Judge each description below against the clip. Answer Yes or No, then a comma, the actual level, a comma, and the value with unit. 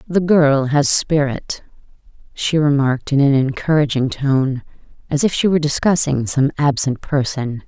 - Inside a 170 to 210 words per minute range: No, average, 140 wpm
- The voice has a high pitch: No, medium, 140 Hz